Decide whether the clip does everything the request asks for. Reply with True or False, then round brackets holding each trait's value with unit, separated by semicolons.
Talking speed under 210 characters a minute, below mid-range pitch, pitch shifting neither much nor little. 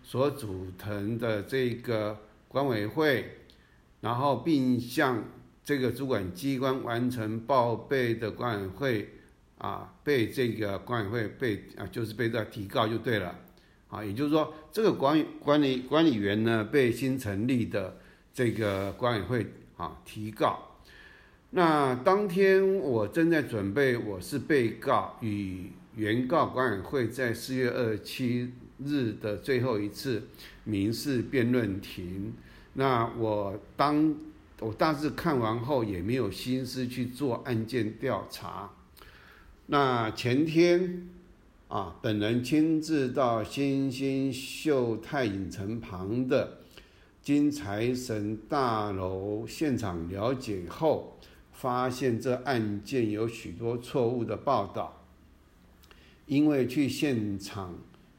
True (180 characters per minute; 115 Hz; 4.6 semitones)